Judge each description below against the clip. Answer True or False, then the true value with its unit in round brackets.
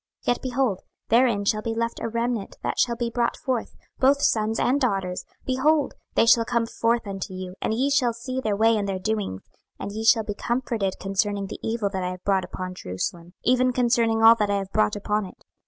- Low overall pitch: False (225 Hz)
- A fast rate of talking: True (220 wpm)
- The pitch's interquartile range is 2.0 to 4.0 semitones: True (3.4 semitones)